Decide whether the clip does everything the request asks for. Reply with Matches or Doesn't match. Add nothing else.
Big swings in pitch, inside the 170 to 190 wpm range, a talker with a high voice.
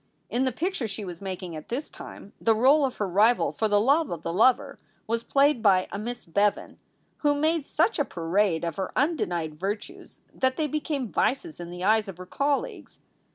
Doesn't match